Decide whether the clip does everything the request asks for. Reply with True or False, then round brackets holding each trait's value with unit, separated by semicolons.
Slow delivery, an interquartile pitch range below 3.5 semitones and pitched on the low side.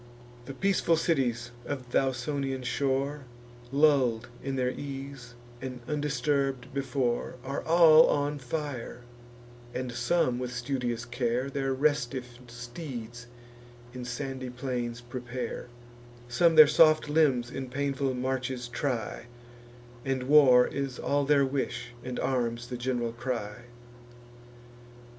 True (115 wpm; 2.5 semitones; 130 Hz)